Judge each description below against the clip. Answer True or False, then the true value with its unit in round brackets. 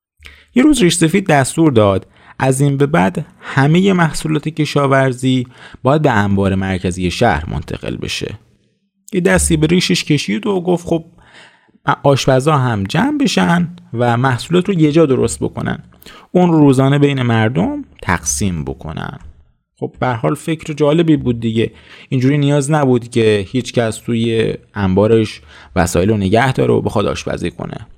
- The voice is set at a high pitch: False (135 Hz)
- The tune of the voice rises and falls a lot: True (6.7 semitones)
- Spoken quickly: False (145 wpm)